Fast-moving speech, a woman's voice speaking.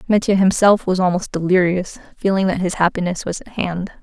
No: average, 180 wpm; female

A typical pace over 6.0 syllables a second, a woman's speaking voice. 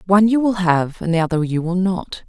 No: 5.7 syllables/s; female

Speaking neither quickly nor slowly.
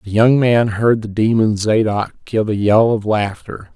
Yes: average, 190 wpm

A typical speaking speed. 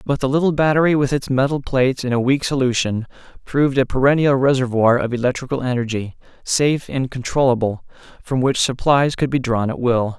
Yes: average, 175 wpm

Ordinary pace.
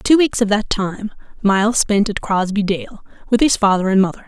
No: fast, 210 wpm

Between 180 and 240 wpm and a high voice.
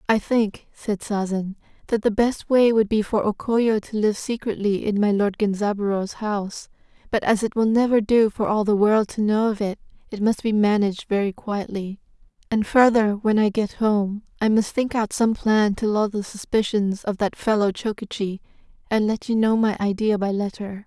Yes: average, 200 wpm; high, 210 Hz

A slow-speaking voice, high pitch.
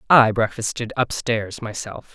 No: slow, 110 wpm; low, 115 Hz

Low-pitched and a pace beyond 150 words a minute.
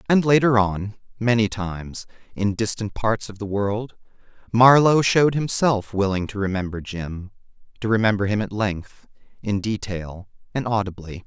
No: low, 105 Hz; average, 145 wpm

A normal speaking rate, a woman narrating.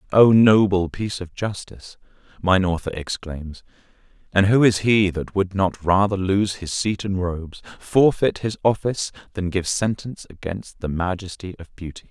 No: average, 160 wpm; male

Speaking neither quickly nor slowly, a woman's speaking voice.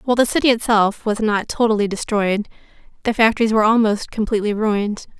Yes: average, 160 wpm; female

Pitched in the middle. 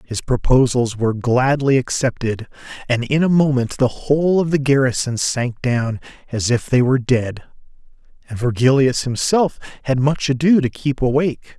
No: low, 130 Hz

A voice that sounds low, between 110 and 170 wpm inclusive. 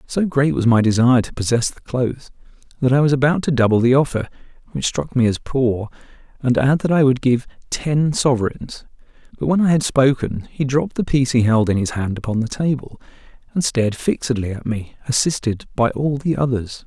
No: low, 130 Hz; fast, 205 wpm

